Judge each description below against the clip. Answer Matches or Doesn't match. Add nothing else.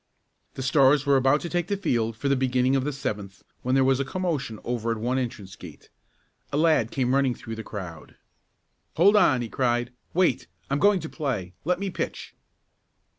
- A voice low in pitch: Matches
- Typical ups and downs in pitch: Matches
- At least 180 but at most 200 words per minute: Matches